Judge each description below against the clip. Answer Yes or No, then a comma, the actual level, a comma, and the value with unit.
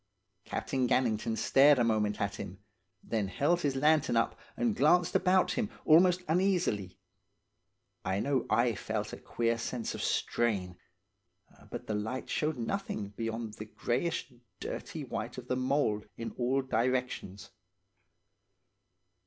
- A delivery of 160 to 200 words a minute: No, slow, 135 wpm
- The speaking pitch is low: Yes, low, 120 Hz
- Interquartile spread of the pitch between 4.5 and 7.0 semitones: Yes, wide, 5.4 semitones